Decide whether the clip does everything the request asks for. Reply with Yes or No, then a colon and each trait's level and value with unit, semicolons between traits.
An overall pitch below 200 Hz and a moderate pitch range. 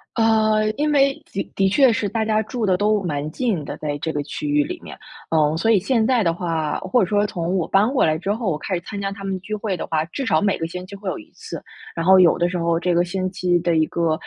Yes: high, 190 Hz; average, 4.4 semitones